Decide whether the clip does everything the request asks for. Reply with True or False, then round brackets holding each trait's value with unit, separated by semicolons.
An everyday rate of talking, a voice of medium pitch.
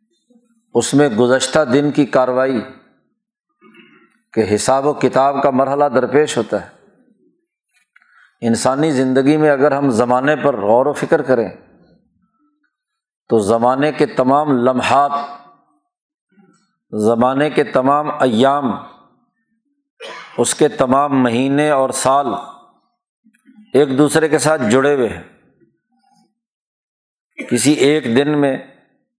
False (105 wpm; 145 Hz)